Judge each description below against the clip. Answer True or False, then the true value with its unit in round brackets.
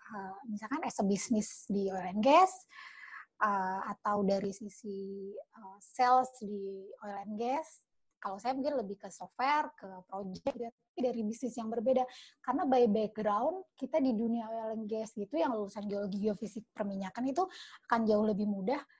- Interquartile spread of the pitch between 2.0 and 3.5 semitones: False (4.1 semitones)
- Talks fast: True (160 wpm)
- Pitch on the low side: False (220 Hz)